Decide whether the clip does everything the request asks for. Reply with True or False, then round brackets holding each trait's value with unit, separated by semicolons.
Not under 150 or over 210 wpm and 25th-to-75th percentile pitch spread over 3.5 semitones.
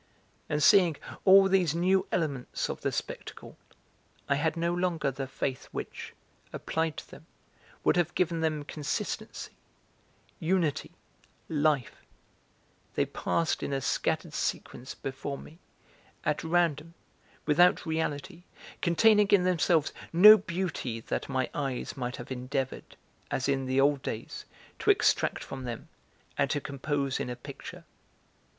False (135 wpm; 4.2 semitones)